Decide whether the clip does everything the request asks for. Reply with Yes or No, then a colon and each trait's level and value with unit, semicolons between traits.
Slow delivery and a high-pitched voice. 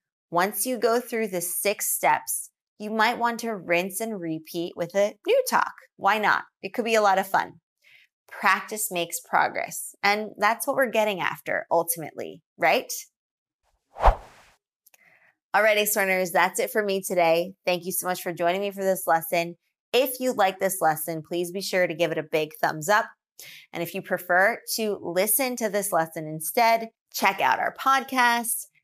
No: average, 175 wpm; high, 195 Hz